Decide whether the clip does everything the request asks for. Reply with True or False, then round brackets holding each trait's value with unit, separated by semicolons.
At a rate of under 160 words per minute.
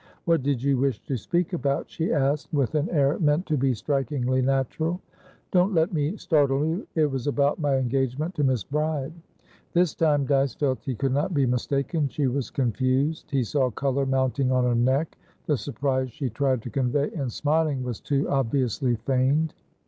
False (185 wpm)